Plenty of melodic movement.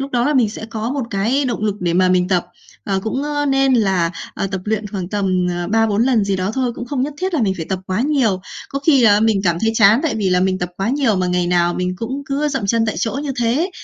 Yes: wide, 6.0 semitones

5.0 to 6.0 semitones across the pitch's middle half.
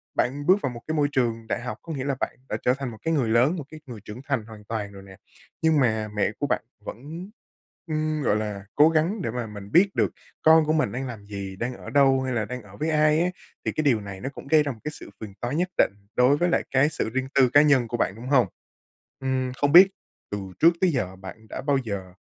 Yes: wide, 5.6 semitones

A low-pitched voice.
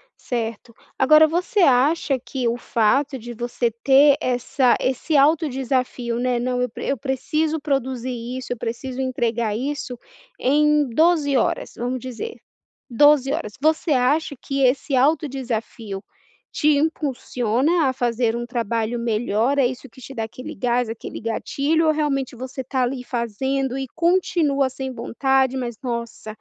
No: very high, 260 Hz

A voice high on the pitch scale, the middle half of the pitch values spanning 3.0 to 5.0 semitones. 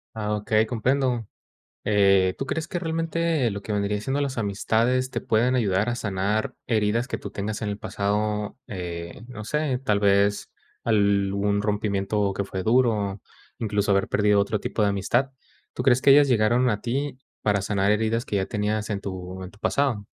No: low, 105 Hz; average, 3.3 semitones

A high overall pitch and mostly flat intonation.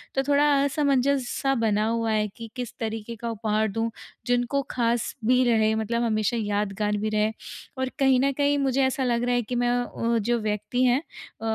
No: high, 235 Hz; average, 3.0 semitones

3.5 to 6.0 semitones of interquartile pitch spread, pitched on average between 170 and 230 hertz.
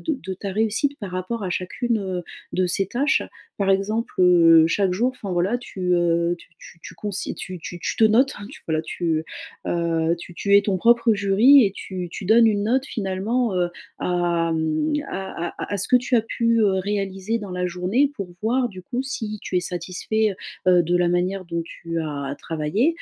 Yes: average, 4.1 semitones; high, 190 Hz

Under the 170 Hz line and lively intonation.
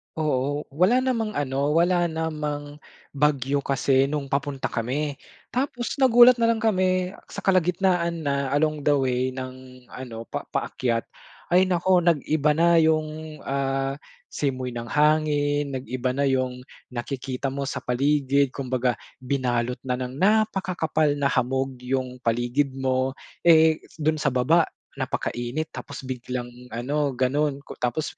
No: medium, 140 Hz; average, 3.6 semitones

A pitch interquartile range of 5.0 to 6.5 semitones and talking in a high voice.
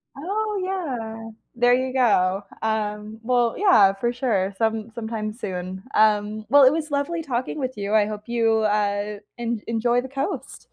No: average, 3.6 semitones; high, 225 Hz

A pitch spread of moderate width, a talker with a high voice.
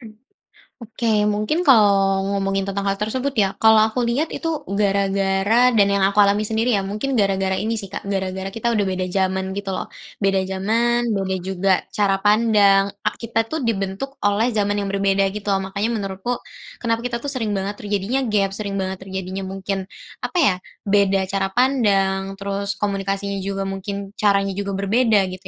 No: narrow, 1.9 semitones; high, 200 Hz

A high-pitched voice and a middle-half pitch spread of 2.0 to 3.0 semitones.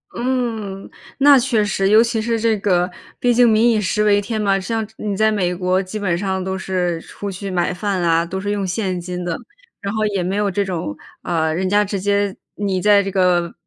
Yes: high, 200 Hz; average, 2.7 semitones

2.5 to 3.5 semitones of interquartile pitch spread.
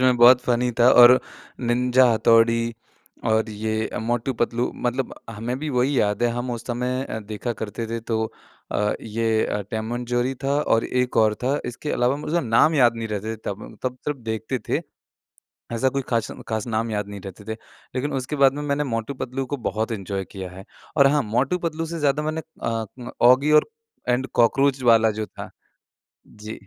Yes: average, 2.9 semitones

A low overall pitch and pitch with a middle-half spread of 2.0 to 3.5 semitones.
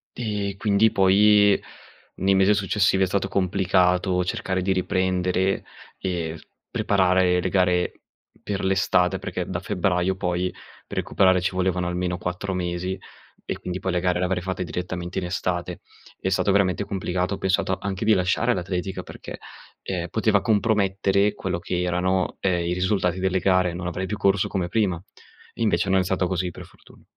No: very low, 95 Hz; narrow, 1.4 semitones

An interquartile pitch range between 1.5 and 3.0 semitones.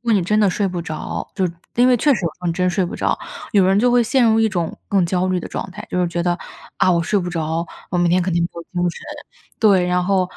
Yes: narrow, 2.6 semitones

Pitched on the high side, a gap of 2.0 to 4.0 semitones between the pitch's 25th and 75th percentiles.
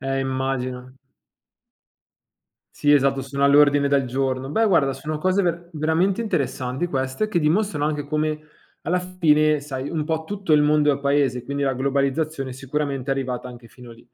No: medium, 140 Hz; average, 2.7 semitones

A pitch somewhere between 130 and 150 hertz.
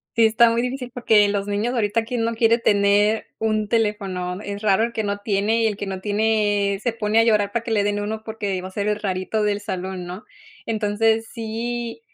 No: high, 210 Hz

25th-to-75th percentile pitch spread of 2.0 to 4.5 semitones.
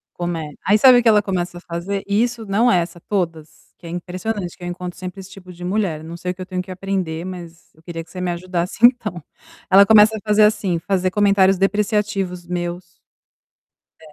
Yes: average, 2.7 semitones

